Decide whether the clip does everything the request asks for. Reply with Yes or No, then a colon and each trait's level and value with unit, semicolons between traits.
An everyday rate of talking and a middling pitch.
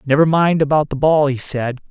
No: fast, 220 wpm; medium, 145 Hz